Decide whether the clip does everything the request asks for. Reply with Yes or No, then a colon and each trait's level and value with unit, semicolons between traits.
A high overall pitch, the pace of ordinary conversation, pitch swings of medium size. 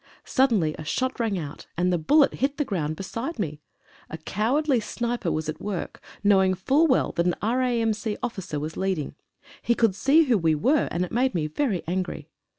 No: high, 205 Hz; average, 190 wpm; wide, 6.8 semitones